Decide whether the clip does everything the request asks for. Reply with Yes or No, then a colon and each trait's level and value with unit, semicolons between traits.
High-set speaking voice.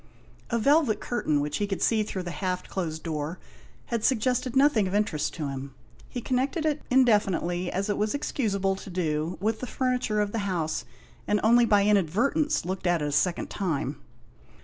Yes: high, 200 Hz